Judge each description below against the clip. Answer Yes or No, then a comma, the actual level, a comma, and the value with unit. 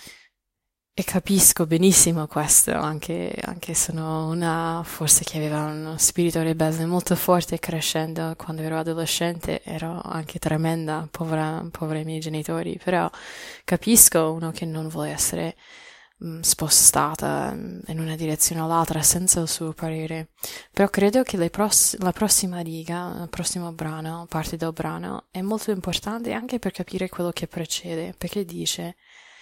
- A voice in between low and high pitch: Yes, medium, 165 Hz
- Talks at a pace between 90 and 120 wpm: No, average, 145 wpm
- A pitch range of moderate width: No, narrow, 2.0 semitones